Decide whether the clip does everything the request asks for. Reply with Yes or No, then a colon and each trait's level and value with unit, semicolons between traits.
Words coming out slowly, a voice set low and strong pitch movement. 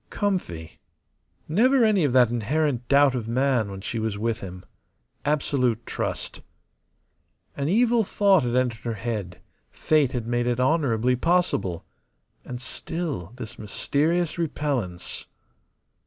Yes: slow, 125 wpm; low, 125 Hz; wide, 5.7 semitones